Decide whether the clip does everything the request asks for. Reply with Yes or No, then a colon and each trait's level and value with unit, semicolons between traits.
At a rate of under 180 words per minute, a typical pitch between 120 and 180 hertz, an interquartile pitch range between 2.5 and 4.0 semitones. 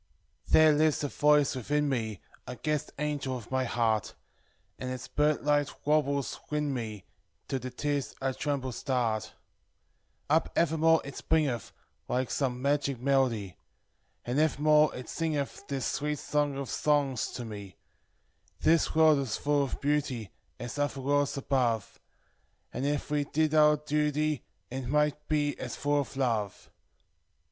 Yes: average, 150 wpm; medium, 140 Hz; average, 2.8 semitones